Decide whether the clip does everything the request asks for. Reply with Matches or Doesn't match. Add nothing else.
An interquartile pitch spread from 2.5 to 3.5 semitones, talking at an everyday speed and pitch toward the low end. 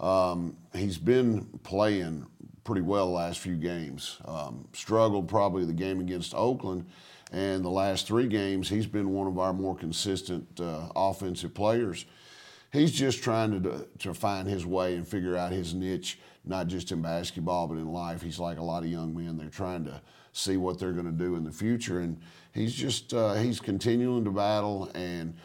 Matches